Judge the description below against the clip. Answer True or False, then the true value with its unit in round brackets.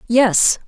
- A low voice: False (230 Hz)